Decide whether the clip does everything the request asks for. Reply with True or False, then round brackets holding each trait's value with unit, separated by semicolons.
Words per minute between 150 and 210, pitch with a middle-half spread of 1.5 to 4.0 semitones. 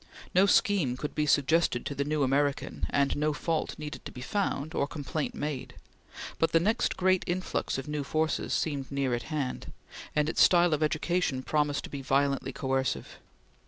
True (180 wpm; 2.7 semitones)